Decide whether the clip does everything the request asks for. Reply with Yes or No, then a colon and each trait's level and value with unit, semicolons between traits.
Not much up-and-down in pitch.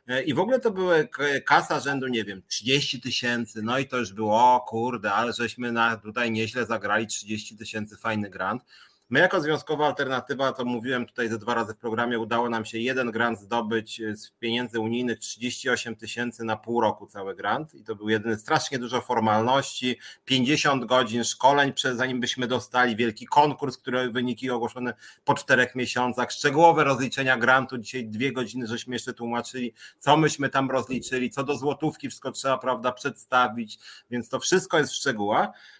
Yes: narrow, 2.3 semitones